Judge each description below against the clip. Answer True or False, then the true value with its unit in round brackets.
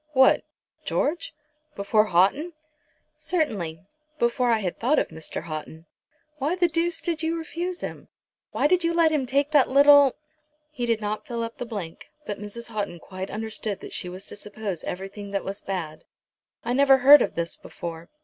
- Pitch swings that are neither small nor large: False (7.3 semitones)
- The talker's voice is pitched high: True (230 Hz)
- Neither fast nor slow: True (180 wpm)